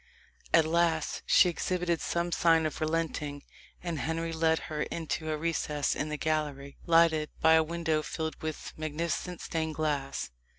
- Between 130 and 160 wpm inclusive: Yes, average, 155 wpm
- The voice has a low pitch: No, medium, 160 Hz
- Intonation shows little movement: Yes, narrow, 1.5 semitones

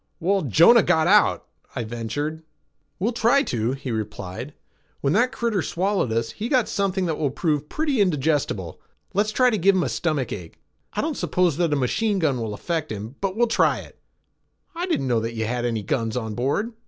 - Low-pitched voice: No, medium, 155 Hz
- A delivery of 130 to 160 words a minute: No, average, 200 wpm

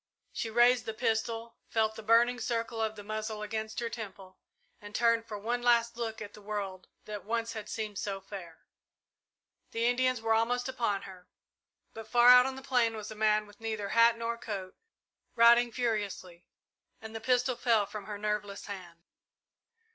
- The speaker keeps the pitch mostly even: Yes, narrow, 2.2 semitones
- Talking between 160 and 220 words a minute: Yes, average, 180 wpm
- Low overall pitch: No, high, 220 Hz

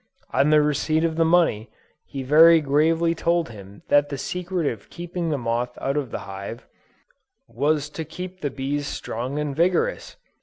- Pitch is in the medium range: Yes, medium, 150 Hz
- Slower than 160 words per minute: No, average, 175 wpm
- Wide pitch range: No, average, 3.8 semitones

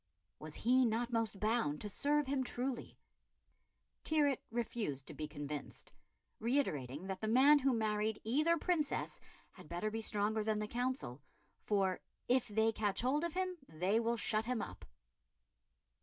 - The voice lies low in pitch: No, high, 225 Hz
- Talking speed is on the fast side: No, average, 155 wpm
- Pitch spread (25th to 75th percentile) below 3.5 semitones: No, average, 4.2 semitones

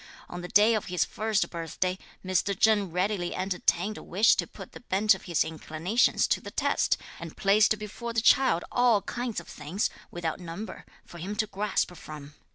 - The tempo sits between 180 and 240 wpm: Yes, average, 185 wpm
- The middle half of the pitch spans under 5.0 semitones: Yes, average, 3.7 semitones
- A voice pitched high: Yes, high, 195 Hz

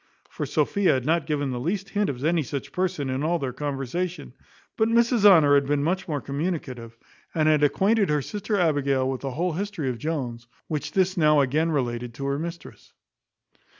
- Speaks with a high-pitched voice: No, medium, 150 Hz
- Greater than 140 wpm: Yes, average, 190 wpm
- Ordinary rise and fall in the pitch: Yes, average, 4.7 semitones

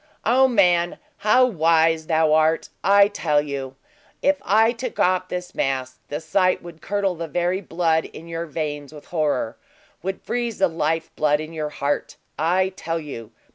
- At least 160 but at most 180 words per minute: Yes, average, 165 wpm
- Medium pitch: Yes, medium, 165 Hz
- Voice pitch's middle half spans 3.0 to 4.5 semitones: Yes, average, 3.6 semitones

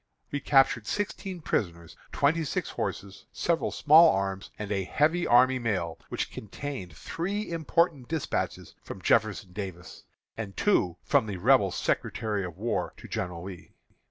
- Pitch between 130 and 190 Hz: No, low, 110 Hz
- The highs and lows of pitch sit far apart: Yes, wide, 8.3 semitones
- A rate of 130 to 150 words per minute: Yes, average, 145 wpm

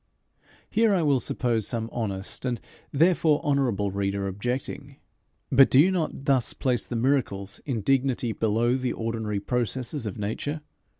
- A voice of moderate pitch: No, low, 125 Hz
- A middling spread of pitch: Yes, average, 4.2 semitones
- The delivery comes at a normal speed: Yes, average, 145 wpm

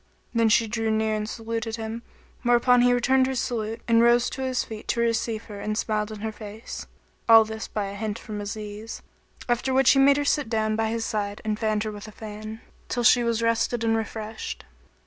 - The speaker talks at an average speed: No, fast, 220 wpm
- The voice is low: No, high, 225 Hz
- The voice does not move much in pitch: Yes, narrow, 1.6 semitones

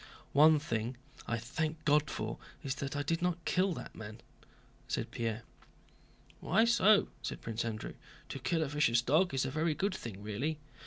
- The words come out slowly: No, average, 175 wpm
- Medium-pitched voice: Yes, medium, 145 Hz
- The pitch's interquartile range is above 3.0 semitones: Yes, wide, 5.5 semitones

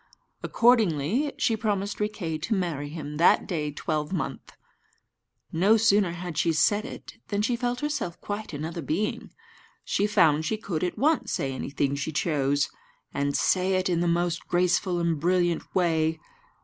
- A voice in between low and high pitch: Yes, medium, 175 Hz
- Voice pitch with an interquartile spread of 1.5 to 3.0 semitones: No, average, 4.8 semitones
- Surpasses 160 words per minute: No, average, 155 wpm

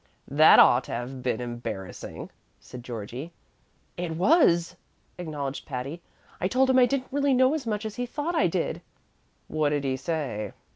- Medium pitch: Yes, medium, 155 Hz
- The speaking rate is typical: Yes, average, 165 wpm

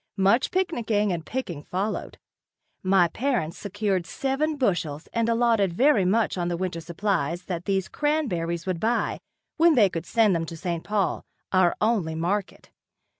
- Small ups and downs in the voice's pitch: No, average, 5.1 semitones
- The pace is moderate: Yes, average, 155 wpm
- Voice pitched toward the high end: Yes, high, 195 Hz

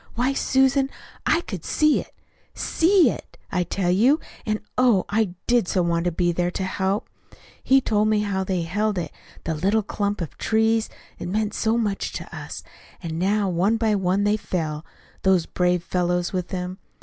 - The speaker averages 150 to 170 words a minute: No, average, 185 wpm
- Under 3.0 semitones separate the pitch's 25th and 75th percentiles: No, average, 3.7 semitones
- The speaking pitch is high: Yes, high, 200 Hz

